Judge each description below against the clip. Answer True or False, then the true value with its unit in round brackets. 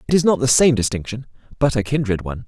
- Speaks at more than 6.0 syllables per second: True (7.1 syllables/s)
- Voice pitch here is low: True (120 Hz)